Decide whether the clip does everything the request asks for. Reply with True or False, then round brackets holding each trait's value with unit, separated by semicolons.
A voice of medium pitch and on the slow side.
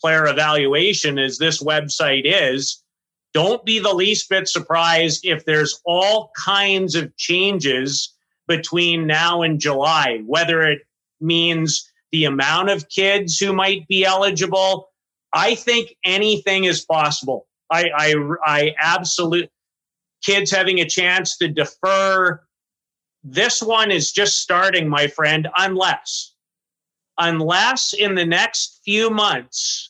True (175 Hz; 125 wpm)